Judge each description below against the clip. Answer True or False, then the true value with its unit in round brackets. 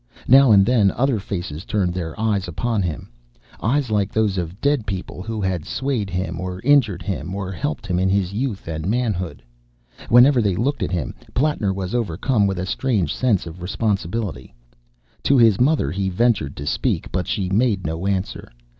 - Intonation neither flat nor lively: True (4.4 semitones)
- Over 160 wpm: True (180 wpm)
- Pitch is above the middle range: False (100 Hz)